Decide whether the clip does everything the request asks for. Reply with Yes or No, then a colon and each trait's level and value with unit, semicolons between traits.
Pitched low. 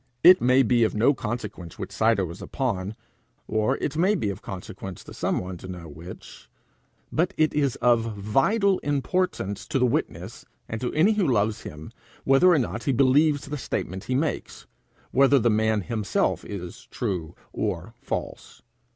Yes: low, 120 Hz